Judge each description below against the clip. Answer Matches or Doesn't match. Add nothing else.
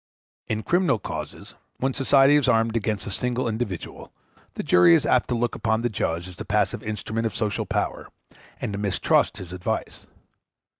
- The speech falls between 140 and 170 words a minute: Doesn't match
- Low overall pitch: Matches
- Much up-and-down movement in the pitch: Doesn't match